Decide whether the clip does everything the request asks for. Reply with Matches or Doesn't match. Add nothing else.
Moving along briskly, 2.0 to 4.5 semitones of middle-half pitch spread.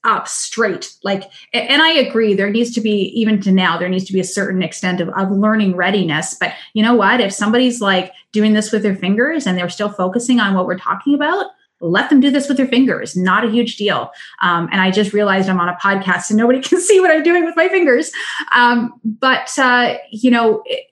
Doesn't match